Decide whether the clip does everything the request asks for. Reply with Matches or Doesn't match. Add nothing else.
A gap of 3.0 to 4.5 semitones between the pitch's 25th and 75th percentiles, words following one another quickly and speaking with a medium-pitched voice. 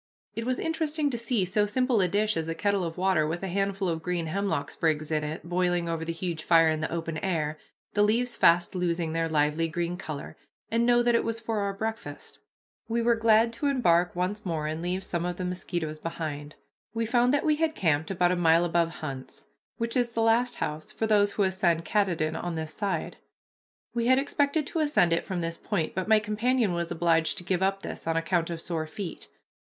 Doesn't match